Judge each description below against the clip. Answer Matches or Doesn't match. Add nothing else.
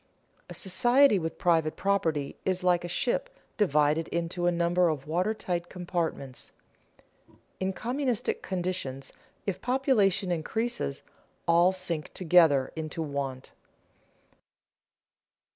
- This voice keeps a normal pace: Doesn't match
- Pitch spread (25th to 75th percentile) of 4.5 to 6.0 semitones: Doesn't match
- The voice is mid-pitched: Matches